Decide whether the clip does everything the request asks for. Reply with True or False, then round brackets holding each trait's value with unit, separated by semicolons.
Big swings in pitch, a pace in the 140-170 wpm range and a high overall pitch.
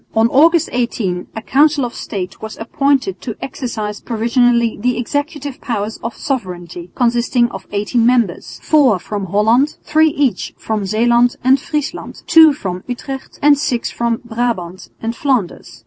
False (4.1 semitones; 145 wpm; 240 Hz)